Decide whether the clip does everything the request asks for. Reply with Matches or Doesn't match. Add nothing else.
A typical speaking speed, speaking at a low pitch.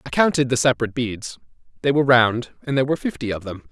Doesn't match